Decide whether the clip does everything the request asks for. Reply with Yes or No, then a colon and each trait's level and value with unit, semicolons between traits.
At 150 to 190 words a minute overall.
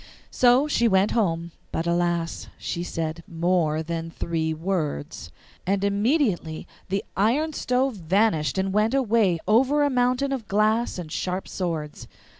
No: average, 140 wpm